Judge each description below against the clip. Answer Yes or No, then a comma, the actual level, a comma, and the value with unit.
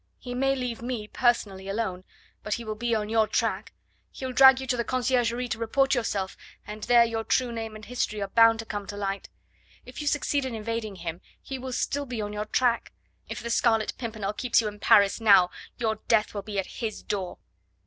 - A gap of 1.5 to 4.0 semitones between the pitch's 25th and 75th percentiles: Yes, average, 2.9 semitones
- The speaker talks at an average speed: No, fast, 215 wpm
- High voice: Yes, high, 225 Hz